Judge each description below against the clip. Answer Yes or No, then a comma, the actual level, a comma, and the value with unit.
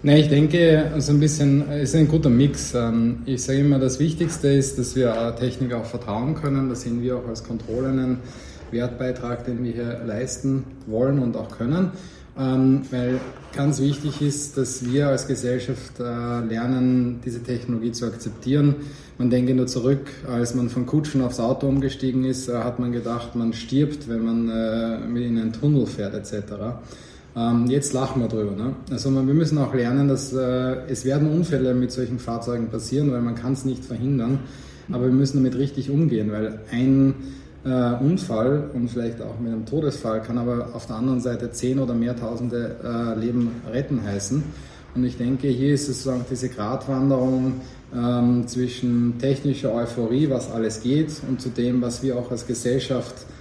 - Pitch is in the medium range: No, low, 125 Hz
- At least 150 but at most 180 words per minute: Yes, average, 175 wpm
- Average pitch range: No, narrow, 2.2 semitones